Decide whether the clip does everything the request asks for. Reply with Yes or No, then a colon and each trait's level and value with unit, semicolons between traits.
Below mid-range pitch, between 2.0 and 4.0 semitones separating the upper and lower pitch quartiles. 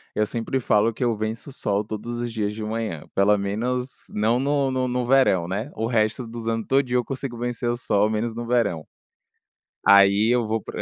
Yes: low, 115 Hz; narrow, 2.6 semitones